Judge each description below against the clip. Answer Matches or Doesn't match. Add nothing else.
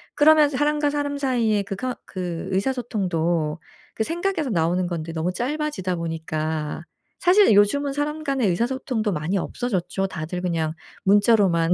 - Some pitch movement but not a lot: Doesn't match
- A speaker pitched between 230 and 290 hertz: Doesn't match